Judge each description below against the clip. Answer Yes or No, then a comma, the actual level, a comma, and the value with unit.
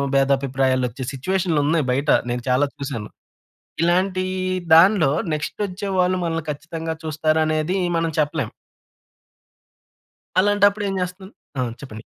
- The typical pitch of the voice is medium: Yes, medium, 160 Hz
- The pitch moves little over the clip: No, average, 5.0 semitones